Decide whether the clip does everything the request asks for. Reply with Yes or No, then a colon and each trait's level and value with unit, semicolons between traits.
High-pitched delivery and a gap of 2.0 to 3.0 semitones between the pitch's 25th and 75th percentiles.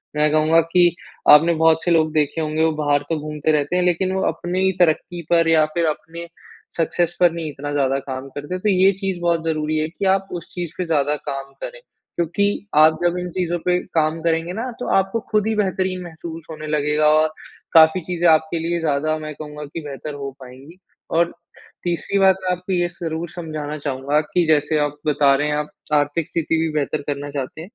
No: medium, 160 Hz; average, 2.7 semitones